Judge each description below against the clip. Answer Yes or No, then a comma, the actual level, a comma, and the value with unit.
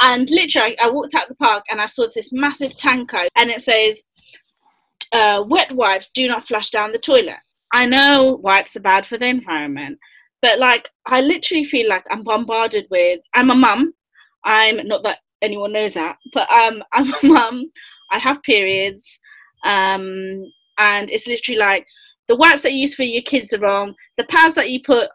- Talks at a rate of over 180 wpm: Yes, average, 190 wpm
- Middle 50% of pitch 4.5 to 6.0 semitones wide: Yes, average, 4.9 semitones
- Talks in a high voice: Yes, high, 240 Hz